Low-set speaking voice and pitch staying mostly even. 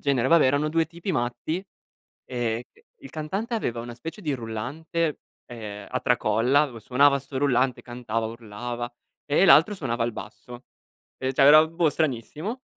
No: low, 130 Hz; average, 4.6 semitones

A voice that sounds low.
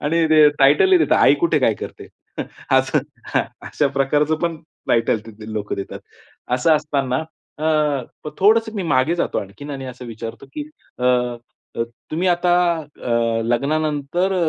No: medium, 145 Hz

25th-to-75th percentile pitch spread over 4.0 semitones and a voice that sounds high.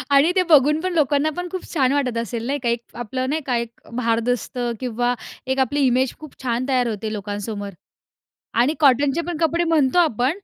Yes: average, 4.4 semitones; very high, 260 Hz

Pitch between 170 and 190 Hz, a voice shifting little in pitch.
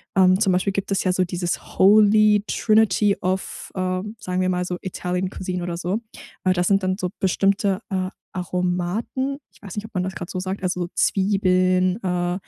Yes: medium, 185 Hz; narrow, 1.6 semitones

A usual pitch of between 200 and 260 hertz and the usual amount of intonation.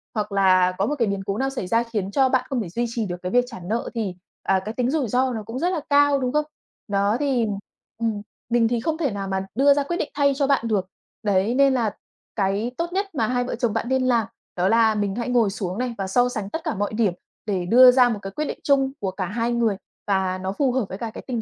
Yes: high, 230 Hz; average, 4.6 semitones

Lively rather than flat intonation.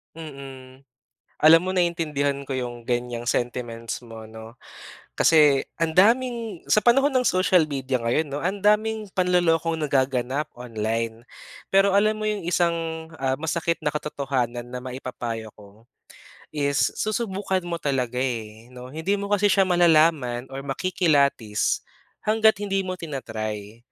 Yes: wide, 6.8 semitones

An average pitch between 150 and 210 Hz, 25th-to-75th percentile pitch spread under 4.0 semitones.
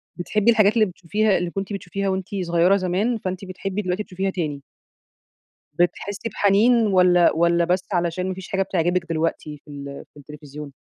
Yes: medium, 185 Hz; narrow, 2.5 semitones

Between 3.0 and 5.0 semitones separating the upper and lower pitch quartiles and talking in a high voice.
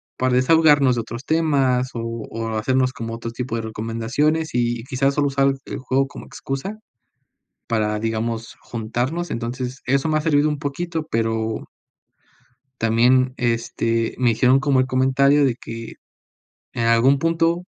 No: average, 3.4 semitones; low, 130 Hz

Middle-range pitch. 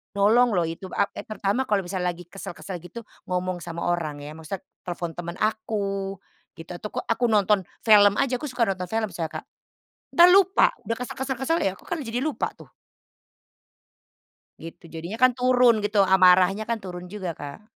No: high, 200 Hz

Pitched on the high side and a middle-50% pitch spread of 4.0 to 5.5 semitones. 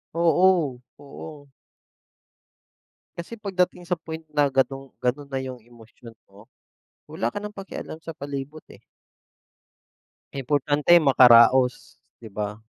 No: medium, 140 Hz; average, 4.7 semitones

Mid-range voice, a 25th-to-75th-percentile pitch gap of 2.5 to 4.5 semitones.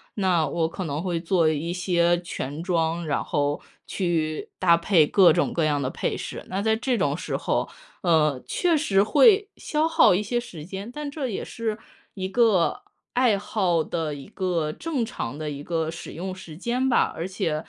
No: medium, 175 Hz; average, 4.9 semitones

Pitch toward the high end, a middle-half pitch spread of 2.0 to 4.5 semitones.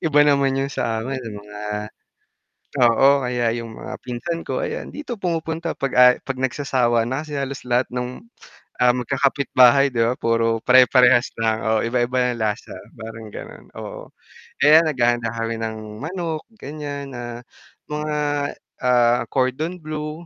No: low, 125 Hz; average, 3.6 semitones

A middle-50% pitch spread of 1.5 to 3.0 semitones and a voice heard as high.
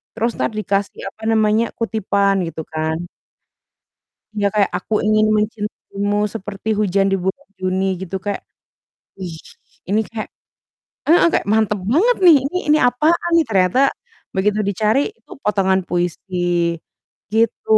Yes: average, 2.7 semitones; high, 205 Hz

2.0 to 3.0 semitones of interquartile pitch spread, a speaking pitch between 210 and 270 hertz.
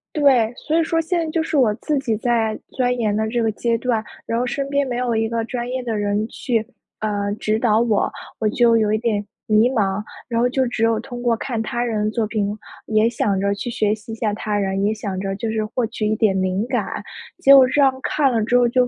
Yes: narrow, 2.6 semitones; high, 230 Hz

